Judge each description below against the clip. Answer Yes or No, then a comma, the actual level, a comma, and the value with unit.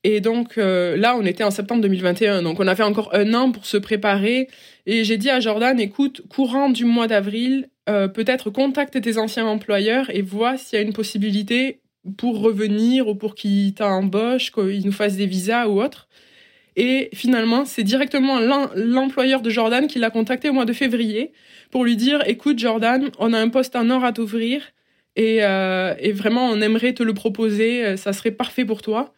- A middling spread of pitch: Yes, average, 3.3 semitones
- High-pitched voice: Yes, high, 225 Hz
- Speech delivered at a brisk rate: No, average, 195 wpm